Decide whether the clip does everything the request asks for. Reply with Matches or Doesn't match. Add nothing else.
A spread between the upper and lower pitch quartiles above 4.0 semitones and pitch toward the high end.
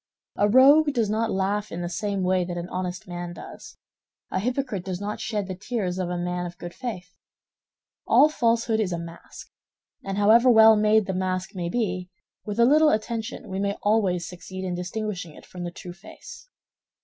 Doesn't match